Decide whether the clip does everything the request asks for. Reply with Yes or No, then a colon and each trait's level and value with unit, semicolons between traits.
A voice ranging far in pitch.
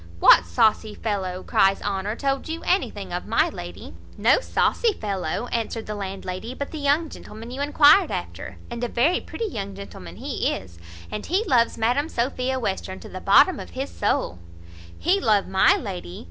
Yes: wide, 6.6 semitones